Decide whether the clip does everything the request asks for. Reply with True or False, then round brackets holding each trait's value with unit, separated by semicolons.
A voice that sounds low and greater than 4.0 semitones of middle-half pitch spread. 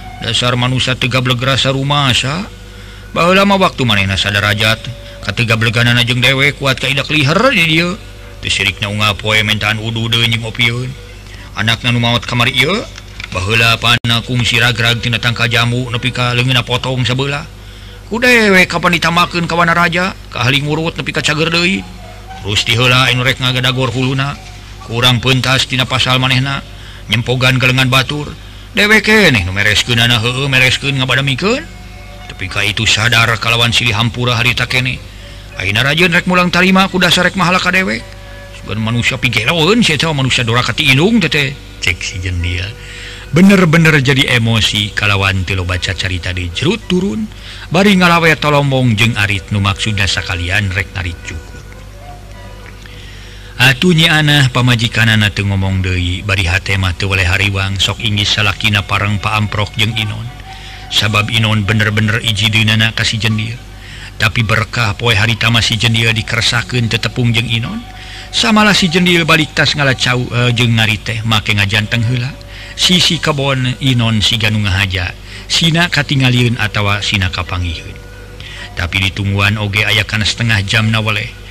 True (115 Hz; 4.5 semitones)